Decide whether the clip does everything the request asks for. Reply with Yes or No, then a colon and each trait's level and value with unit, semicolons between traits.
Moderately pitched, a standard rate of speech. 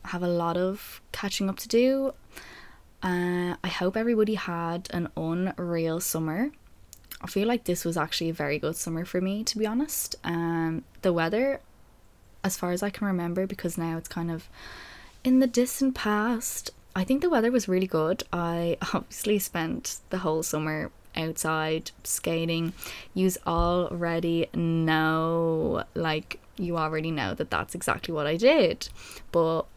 Yes: medium, 175 Hz; average, 155 wpm